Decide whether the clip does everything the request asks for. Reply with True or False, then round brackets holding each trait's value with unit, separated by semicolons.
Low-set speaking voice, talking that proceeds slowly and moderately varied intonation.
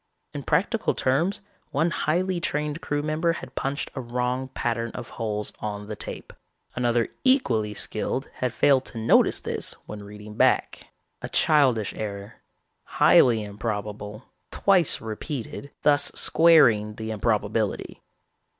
False (120 Hz; 130 wpm; 5.7 semitones)